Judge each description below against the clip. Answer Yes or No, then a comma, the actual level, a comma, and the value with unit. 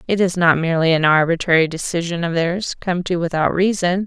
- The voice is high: No, medium, 170 Hz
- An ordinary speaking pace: Yes, average, 190 wpm